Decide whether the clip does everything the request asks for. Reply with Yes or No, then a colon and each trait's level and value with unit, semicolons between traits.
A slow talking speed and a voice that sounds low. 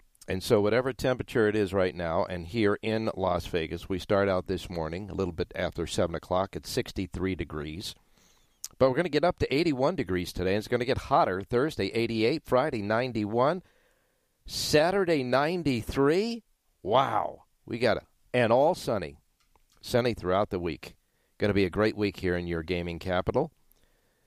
No: average, 175 wpm; low, 105 Hz